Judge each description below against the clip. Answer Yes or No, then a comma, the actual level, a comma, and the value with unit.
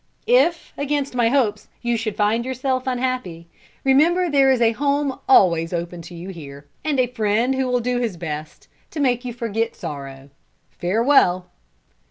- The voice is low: No, high, 235 Hz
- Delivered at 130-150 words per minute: No, average, 165 wpm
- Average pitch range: No, wide, 6.9 semitones